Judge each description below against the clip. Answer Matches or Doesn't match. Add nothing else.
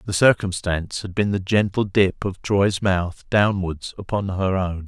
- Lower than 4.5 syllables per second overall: Matches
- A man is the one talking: Matches